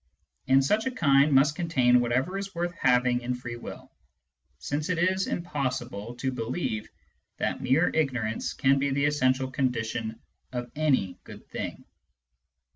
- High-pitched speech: No, low, 135 Hz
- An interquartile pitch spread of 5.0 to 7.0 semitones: No, average, 4.1 semitones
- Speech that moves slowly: No, average, 145 wpm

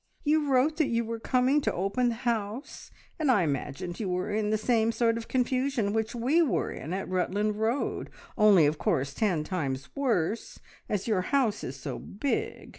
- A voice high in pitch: Yes, high, 220 Hz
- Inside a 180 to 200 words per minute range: Yes, average, 185 wpm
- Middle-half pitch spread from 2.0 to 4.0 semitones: No, average, 5.3 semitones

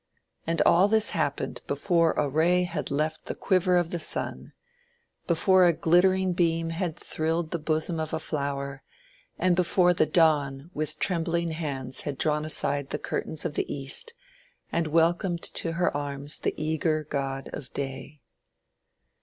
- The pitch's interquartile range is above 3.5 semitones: No, average, 3.1 semitones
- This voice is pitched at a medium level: Yes, medium, 160 Hz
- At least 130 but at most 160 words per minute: Yes, average, 155 wpm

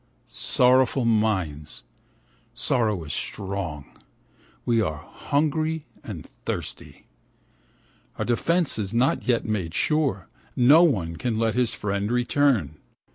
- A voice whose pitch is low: Yes, low, 115 Hz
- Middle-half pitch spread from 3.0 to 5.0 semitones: No, wide, 5.4 semitones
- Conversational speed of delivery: No, slow, 110 wpm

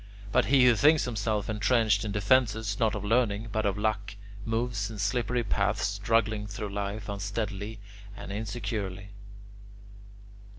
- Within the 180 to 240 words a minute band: No, slow, 135 wpm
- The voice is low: Yes, low, 105 Hz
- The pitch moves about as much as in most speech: No, narrow, 2.0 semitones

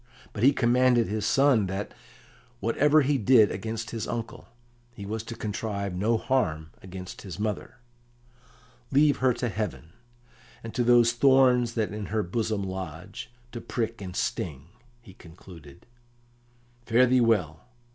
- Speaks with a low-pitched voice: Yes, low, 110 Hz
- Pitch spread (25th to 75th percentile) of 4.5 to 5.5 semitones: No, average, 4.1 semitones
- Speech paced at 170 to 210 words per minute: No, average, 145 wpm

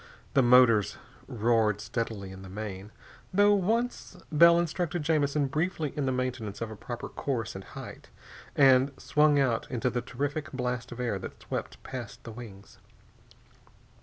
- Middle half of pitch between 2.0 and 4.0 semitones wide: No, average, 4.8 semitones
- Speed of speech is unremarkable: Yes, average, 155 wpm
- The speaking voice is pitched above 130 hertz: No, low, 125 Hz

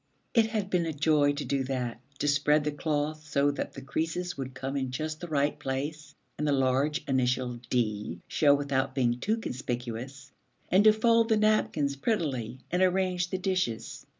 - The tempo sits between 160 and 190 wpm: Yes, average, 180 wpm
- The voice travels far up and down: No, average, 4.8 semitones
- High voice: No, medium, 145 Hz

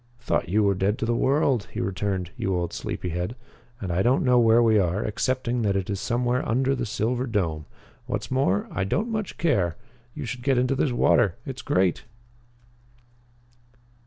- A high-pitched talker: No, low, 115 Hz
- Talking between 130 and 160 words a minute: No, average, 185 wpm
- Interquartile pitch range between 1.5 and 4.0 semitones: No, average, 4.8 semitones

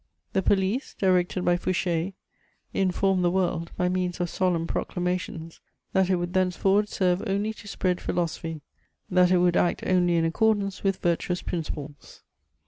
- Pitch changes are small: Yes, narrow, 1.5 semitones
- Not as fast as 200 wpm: Yes, average, 155 wpm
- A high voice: No, medium, 180 Hz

